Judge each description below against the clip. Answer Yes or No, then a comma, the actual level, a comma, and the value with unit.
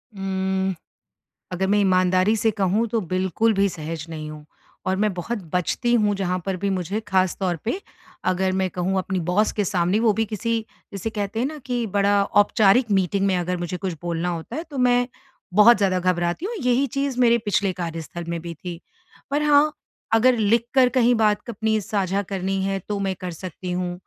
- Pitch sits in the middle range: No, high, 195 Hz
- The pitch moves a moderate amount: Yes, average, 3.5 semitones